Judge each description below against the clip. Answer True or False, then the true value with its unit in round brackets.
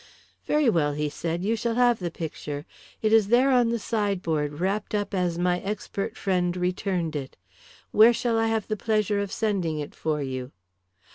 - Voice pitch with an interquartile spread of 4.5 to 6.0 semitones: True (5.0 semitones)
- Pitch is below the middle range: False (195 Hz)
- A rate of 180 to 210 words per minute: True (185 wpm)